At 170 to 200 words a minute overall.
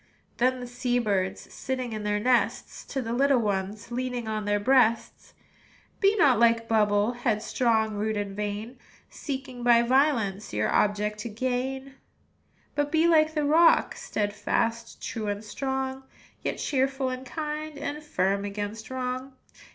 No: average, 150 wpm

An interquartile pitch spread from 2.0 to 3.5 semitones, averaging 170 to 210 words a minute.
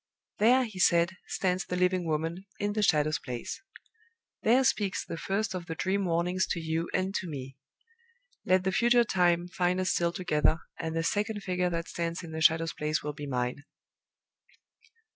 Yes: average, 2.7 semitones; average, 180 wpm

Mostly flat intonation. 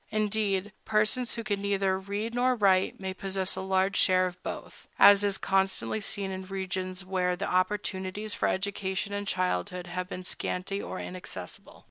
Yes: narrow, 1.6 semitones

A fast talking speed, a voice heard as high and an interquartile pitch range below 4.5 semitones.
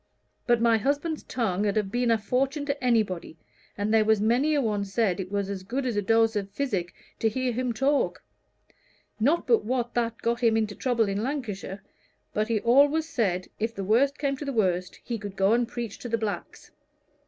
Yes: fast, 210 wpm; high, 230 Hz; average, 3.8 semitones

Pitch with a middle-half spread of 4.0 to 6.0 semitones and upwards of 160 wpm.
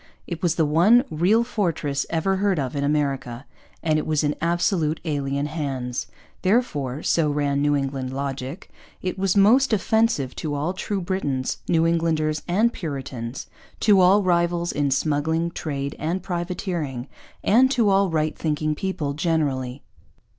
No: average, 4.5 semitones; average, 150 wpm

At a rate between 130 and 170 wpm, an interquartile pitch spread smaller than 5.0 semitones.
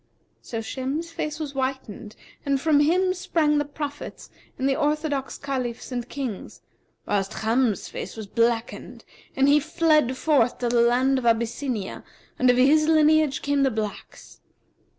Yes: average, 150 wpm; average, 4.0 semitones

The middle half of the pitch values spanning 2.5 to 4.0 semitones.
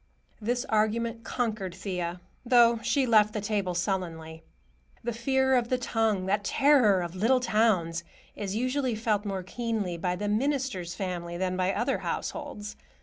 No: average, 4.5 semitones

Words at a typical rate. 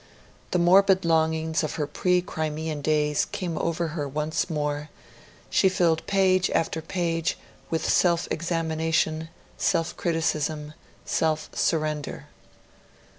No: slow, 115 wpm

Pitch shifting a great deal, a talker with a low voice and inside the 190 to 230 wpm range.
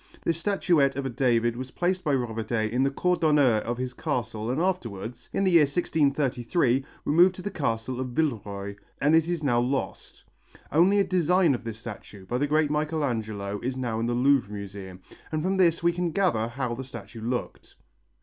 Yes: wide, 5.7 semitones; low, 130 Hz; average, 195 wpm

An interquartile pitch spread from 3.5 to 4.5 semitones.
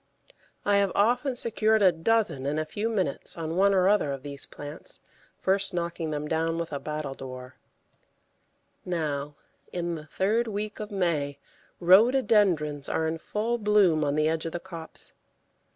No: average, 5.2 semitones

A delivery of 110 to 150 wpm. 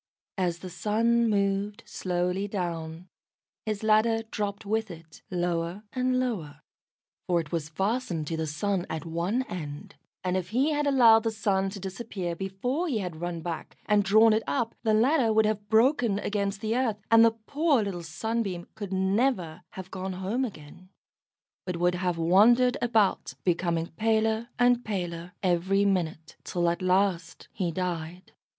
No: average, 160 wpm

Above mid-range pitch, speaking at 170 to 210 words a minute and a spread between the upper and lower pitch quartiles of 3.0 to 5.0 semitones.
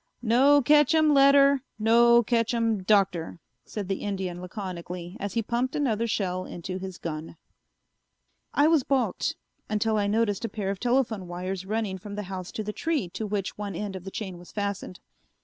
Yes: high, 210 Hz; average, 175 wpm; average, 4.1 semitones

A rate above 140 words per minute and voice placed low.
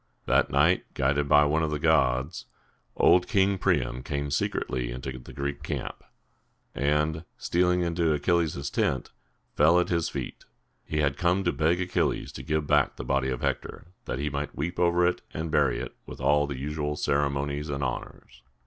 Yes: average, 175 wpm; very low, 75 Hz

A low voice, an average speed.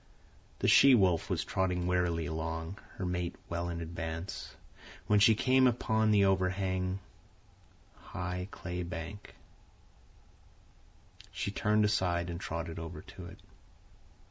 No: very low, 90 Hz; slow, 120 wpm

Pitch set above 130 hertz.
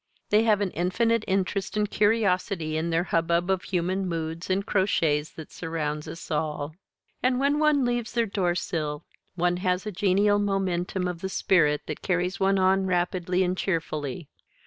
Yes: medium, 185 Hz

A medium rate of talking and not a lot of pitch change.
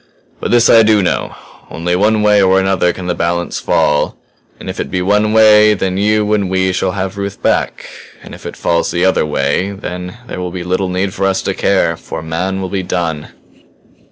No: fast, 215 wpm; narrow, 2.3 semitones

